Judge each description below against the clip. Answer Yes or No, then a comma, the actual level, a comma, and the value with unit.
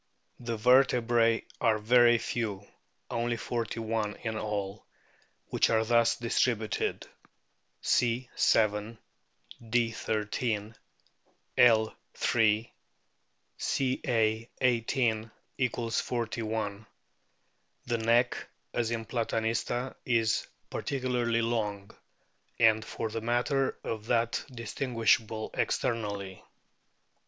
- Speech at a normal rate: No, slow, 90 wpm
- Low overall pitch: Yes, low, 115 Hz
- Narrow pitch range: Yes, narrow, 1.6 semitones